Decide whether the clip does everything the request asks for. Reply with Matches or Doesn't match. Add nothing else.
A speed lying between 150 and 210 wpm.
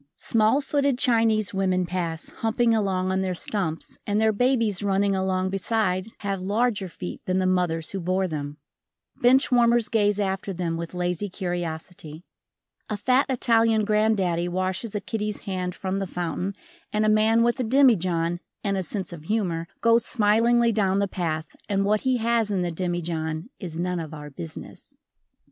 Matches